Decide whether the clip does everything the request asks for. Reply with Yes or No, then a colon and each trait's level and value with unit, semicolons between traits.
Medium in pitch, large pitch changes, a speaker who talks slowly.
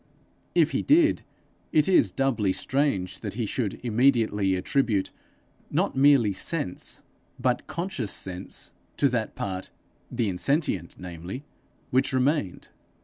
No: low, 120 Hz; wide, 6.4 semitones; slow, 120 wpm